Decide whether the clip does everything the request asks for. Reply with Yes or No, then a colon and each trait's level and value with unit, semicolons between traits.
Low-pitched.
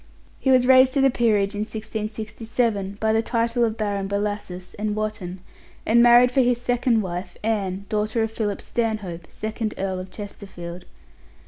No: high, 215 Hz